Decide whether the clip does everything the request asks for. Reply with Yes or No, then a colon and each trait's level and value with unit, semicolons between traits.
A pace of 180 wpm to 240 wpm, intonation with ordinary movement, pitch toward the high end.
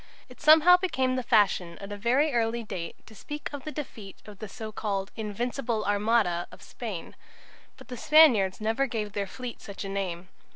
Yes: average, 190 wpm; average, 4.4 semitones; high, 220 Hz